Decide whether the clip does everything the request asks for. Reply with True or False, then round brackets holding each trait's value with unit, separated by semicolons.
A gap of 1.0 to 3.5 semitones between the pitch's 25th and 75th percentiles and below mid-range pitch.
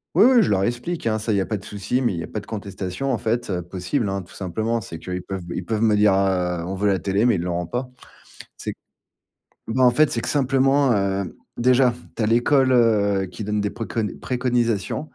False (4.1 semitones; 105 Hz)